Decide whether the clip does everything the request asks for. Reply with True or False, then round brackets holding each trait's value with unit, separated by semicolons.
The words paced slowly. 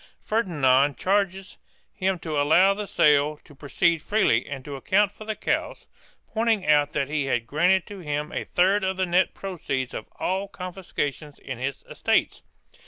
False (170 wpm)